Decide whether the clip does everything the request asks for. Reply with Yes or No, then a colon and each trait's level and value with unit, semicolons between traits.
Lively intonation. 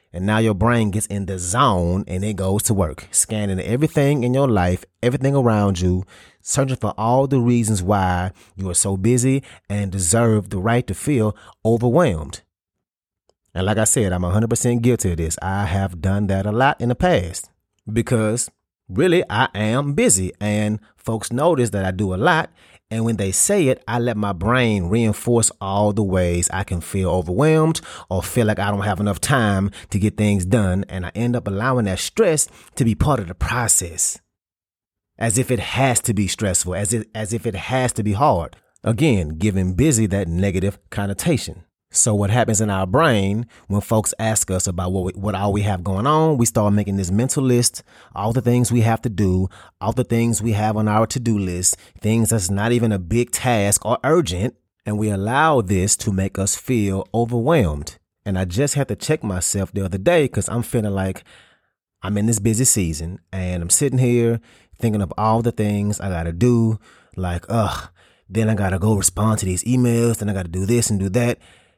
No: average, 3.5 semitones